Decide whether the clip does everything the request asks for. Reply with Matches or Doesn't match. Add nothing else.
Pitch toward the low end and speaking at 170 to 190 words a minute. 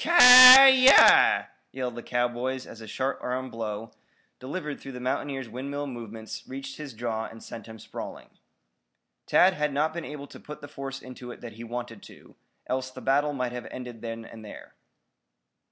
Matches